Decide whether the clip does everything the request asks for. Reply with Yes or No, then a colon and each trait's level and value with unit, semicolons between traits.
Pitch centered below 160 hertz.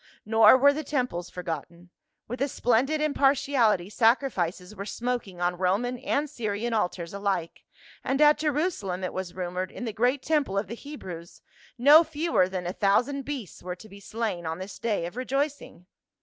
No: high, 220 Hz